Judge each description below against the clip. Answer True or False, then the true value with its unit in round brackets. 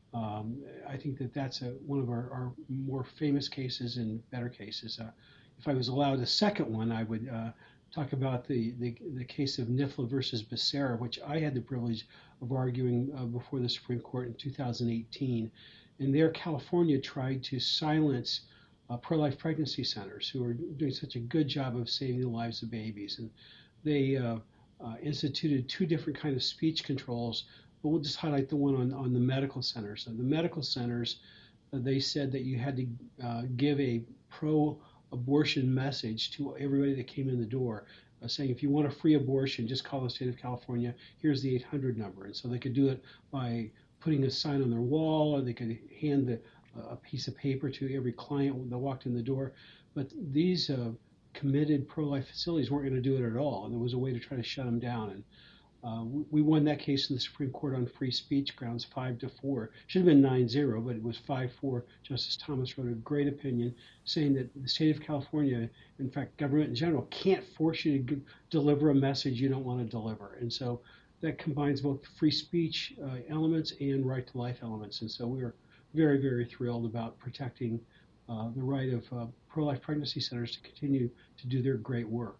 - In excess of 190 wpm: True (205 wpm)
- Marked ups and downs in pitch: False (3.0 semitones)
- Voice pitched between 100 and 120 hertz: False (130 Hz)